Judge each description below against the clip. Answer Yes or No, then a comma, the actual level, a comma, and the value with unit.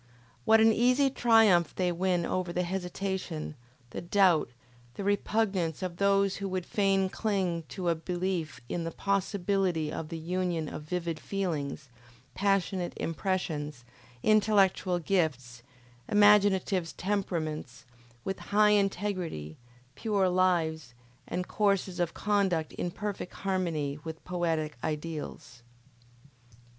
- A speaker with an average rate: No, slow, 115 wpm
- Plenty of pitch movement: No, average, 3.4 semitones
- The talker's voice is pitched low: No, medium, 180 Hz